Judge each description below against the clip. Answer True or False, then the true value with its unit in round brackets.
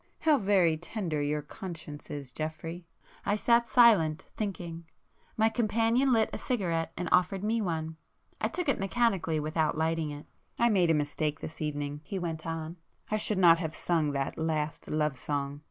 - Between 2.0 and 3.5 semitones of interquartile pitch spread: False (5.1 semitones)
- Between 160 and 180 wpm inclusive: True (165 wpm)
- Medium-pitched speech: True (165 Hz)